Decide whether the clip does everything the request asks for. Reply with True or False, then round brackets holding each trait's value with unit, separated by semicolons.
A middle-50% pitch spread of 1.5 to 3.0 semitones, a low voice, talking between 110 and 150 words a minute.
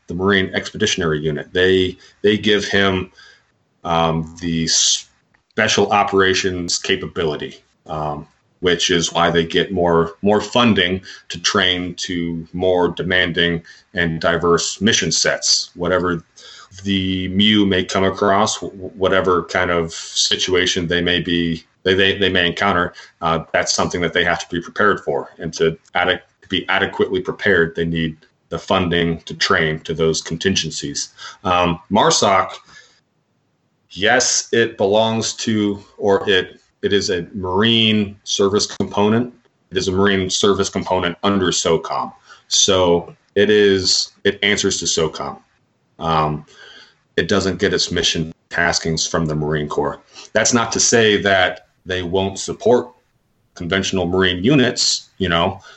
True (2.5 semitones; 90 Hz; 140 wpm)